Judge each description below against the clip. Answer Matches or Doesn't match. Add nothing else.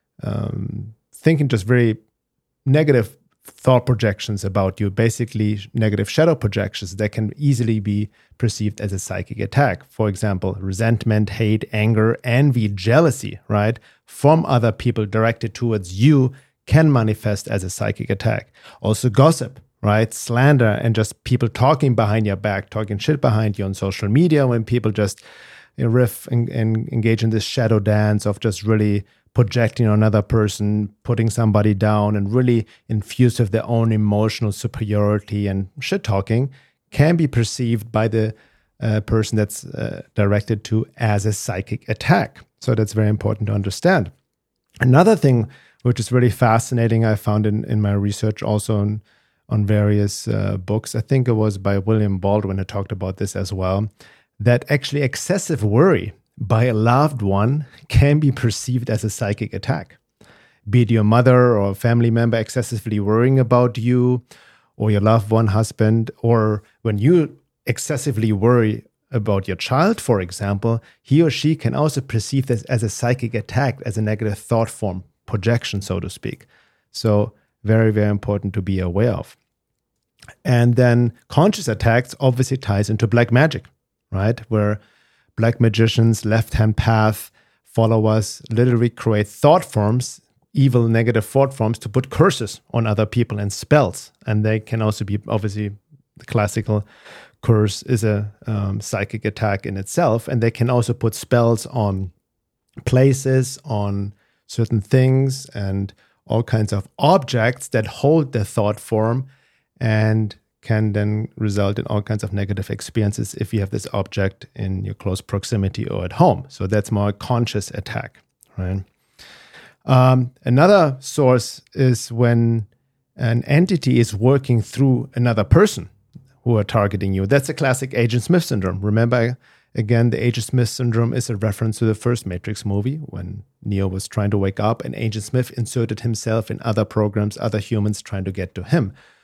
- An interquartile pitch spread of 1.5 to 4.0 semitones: Matches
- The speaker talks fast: Doesn't match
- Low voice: Matches